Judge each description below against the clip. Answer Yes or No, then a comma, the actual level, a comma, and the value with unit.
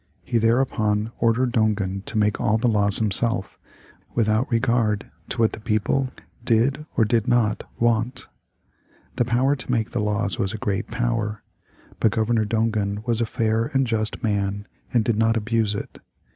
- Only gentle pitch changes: Yes, narrow, 2.0 semitones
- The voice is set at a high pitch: No, low, 110 Hz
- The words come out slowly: No, average, 165 wpm